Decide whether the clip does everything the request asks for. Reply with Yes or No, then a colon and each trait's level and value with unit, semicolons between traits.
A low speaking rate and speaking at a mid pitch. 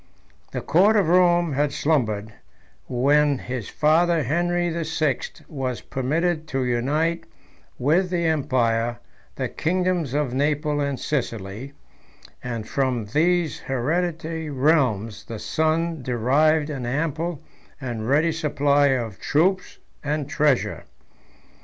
Yes: slow, 115 wpm; medium, 145 Hz